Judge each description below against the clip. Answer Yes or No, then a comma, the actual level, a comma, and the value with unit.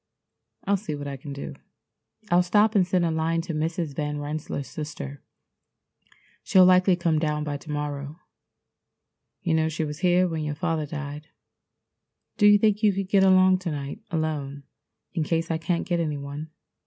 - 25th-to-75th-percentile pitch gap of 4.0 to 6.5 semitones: No, average, 3.5 semitones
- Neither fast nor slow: Yes, average, 180 wpm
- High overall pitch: No, medium, 160 Hz